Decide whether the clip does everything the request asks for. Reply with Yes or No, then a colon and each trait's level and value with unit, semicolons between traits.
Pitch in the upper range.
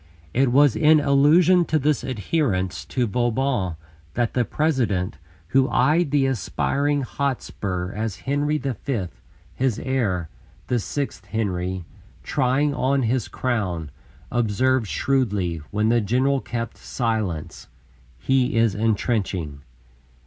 No: low, 125 Hz